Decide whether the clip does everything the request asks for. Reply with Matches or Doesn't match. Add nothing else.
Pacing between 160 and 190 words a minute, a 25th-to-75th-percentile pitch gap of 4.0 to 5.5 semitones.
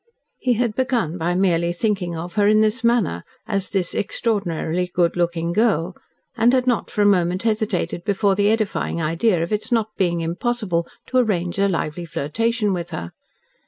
Matches